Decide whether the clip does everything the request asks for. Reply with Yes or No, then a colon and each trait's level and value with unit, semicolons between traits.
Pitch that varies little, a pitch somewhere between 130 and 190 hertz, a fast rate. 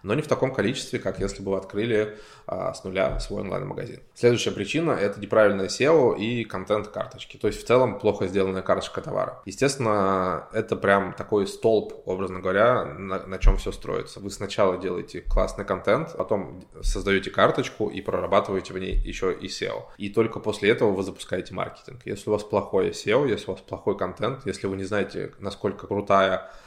No: narrow, 1.8 semitones; low, 100 Hz; fast, 180 wpm